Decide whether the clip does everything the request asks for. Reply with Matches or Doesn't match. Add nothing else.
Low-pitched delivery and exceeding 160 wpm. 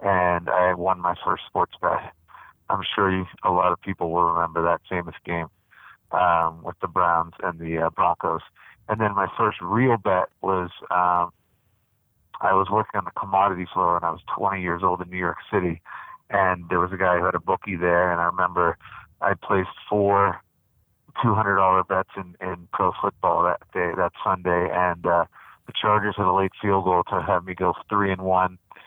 Matches